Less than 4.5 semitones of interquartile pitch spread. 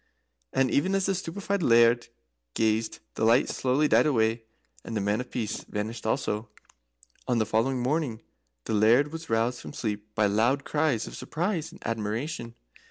No: average, 4.8 semitones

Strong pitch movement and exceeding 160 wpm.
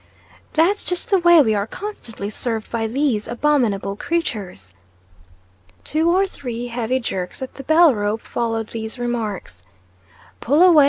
No: wide, 6.4 semitones; average, 145 wpm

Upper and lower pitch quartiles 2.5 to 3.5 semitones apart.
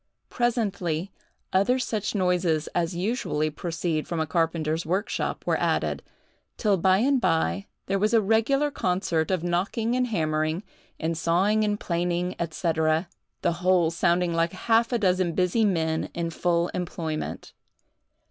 No: average, 3.9 semitones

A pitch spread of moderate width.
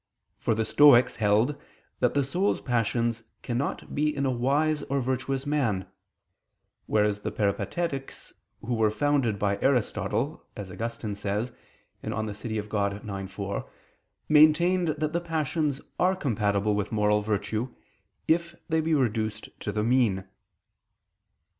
No: wide, 5.7 semitones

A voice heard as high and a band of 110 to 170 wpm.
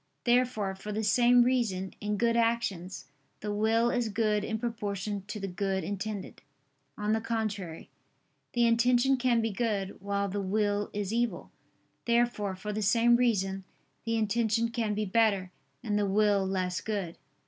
Yes: high, 210 Hz; average, 160 wpm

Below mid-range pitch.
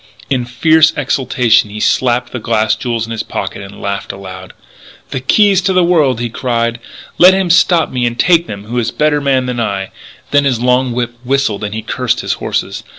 Yes: low, 125 Hz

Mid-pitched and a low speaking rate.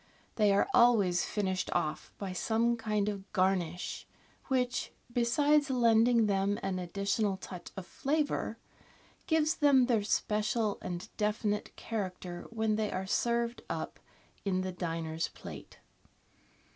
No: high, 210 Hz; slow, 125 wpm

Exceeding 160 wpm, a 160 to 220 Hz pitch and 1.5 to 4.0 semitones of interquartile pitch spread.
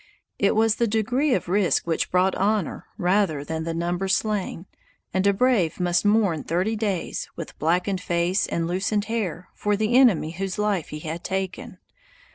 Yes: average, 170 wpm; high, 190 Hz; average, 3.6 semitones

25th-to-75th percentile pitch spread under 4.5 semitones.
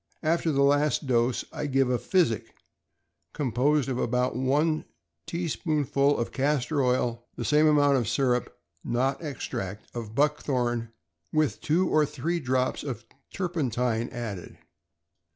Yes: average, 3.7 semitones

